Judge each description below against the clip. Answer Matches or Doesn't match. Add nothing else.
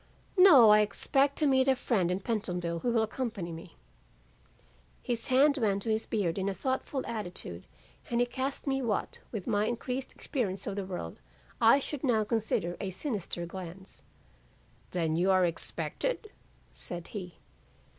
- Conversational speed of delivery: Matches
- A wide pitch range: Matches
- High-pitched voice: Matches